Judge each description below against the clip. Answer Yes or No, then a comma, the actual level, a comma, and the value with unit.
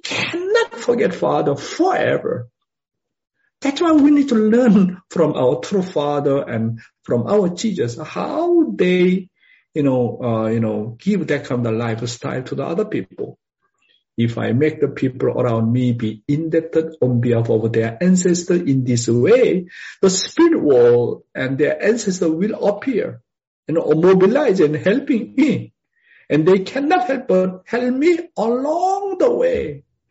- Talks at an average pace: Yes, average, 150 wpm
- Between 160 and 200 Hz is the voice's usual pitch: Yes, medium, 185 Hz